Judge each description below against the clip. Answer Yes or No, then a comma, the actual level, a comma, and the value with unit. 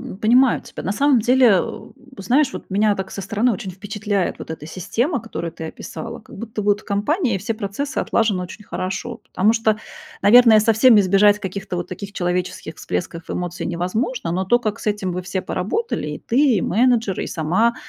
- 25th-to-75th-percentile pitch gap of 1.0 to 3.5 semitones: No, average, 4.1 semitones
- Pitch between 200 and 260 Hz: Yes, high, 210 Hz